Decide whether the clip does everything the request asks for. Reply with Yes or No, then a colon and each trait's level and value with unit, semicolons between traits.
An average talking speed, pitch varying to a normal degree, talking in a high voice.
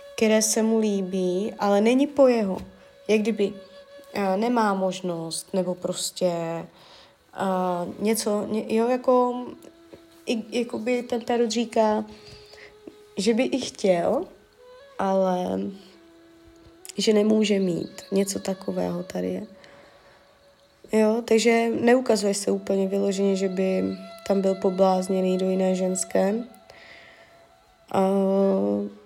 No: slow, 110 wpm; average, 4.0 semitones; high, 200 Hz